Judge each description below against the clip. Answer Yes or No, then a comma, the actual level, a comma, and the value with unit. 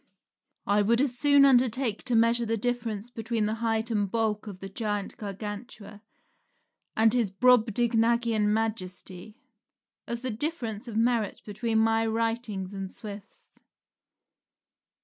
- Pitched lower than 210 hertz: No, high, 225 Hz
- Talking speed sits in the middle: No, slow, 130 wpm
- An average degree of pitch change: No, narrow, 2.2 semitones